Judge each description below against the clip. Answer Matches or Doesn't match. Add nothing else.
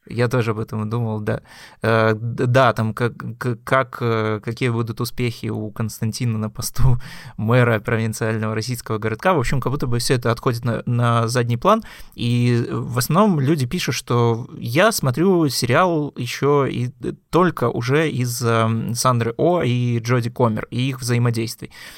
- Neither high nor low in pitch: Doesn't match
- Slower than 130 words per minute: Doesn't match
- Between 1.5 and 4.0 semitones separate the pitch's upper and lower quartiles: Matches